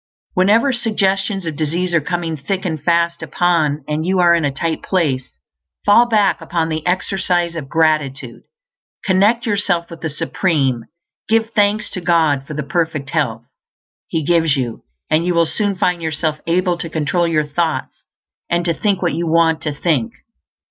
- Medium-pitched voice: Yes, medium, 170 Hz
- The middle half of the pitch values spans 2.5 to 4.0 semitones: Yes, average, 3.1 semitones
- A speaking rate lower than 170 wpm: No, average, 175 wpm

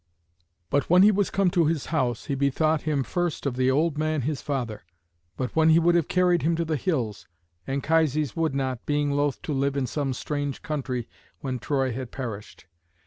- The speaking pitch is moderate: Yes, medium, 145 Hz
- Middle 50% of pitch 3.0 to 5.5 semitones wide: Yes, average, 3.5 semitones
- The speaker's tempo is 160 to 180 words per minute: No, average, 195 wpm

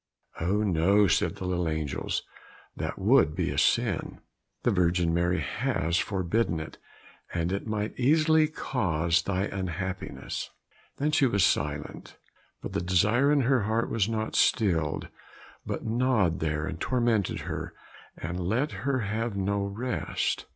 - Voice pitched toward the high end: No, low, 100 Hz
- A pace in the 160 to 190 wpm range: No, average, 145 wpm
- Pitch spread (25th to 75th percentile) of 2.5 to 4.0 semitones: No, average, 5.2 semitones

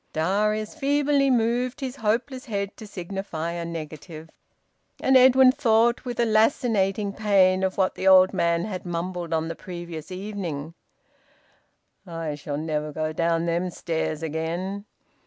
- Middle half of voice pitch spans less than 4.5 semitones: No, average, 5.1 semitones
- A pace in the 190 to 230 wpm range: No, average, 140 wpm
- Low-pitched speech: No, high, 190 Hz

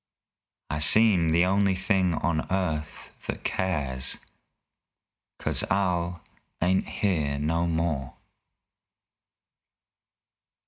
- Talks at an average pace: No, slow, 85 wpm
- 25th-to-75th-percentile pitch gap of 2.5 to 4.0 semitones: Yes, average, 3.5 semitones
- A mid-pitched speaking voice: No, very low, 85 Hz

